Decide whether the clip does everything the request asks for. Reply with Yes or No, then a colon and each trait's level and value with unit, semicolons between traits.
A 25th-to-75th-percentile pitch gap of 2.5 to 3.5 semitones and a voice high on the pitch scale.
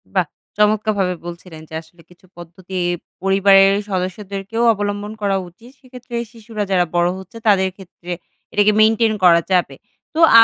Yes: average, 2.8 semitones; high, 195 Hz